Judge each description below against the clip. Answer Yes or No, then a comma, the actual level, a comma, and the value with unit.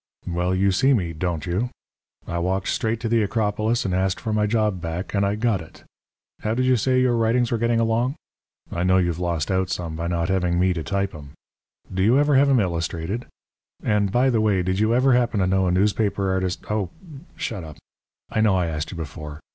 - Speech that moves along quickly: Yes, fast, 220 wpm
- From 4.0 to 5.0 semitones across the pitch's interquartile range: Yes, average, 4.3 semitones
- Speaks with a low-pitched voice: Yes, very low, 95 Hz